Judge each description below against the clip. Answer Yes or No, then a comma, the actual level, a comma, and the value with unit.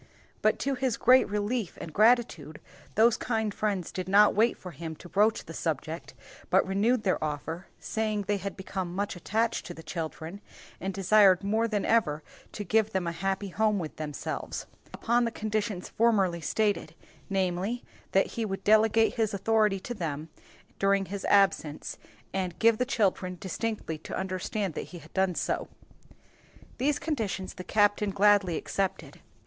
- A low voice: No, high, 200 Hz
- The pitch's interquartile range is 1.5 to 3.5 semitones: Yes, average, 3.1 semitones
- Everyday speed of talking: Yes, average, 165 wpm